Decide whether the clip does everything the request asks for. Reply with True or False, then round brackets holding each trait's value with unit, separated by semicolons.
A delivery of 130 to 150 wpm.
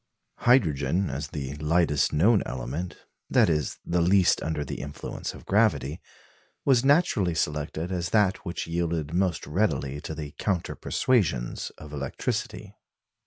True (135 wpm)